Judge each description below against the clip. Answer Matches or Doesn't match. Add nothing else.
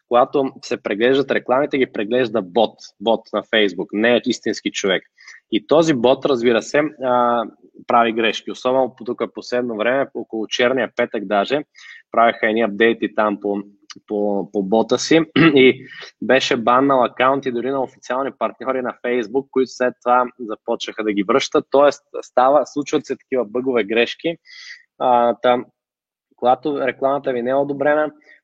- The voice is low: Matches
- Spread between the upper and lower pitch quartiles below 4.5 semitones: Matches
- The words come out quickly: Doesn't match